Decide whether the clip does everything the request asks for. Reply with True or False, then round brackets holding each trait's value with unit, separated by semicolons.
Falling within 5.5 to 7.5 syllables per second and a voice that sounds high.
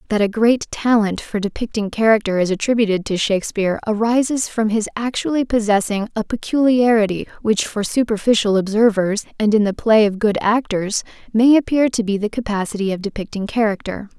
True (5.6 syllables/s; 215 Hz)